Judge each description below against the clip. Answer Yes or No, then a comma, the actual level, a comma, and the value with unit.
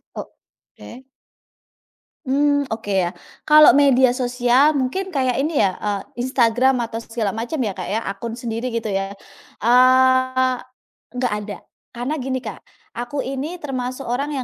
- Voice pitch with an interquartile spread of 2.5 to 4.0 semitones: Yes, average, 2.8 semitones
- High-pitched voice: Yes, very high, 250 Hz